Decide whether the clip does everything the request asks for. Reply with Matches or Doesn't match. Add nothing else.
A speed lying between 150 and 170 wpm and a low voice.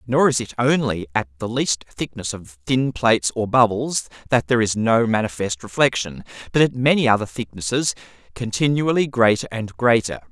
Matches